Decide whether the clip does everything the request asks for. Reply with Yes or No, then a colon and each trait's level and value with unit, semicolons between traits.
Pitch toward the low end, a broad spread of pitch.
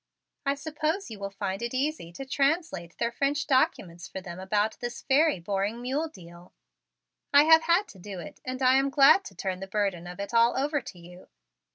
No: high, 235 Hz; wide, 6.9 semitones